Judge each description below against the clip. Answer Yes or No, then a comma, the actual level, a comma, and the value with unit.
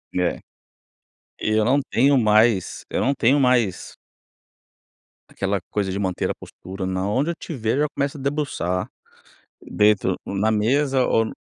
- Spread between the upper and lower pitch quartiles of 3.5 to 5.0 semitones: No, wide, 5.5 semitones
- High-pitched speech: No, low, 110 Hz